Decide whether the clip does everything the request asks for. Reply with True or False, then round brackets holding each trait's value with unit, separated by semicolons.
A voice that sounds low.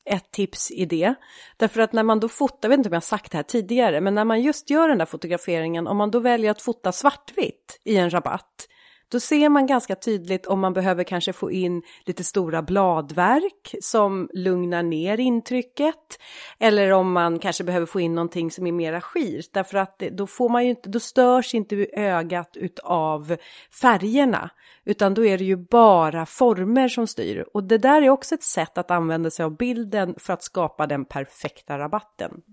False (195 Hz)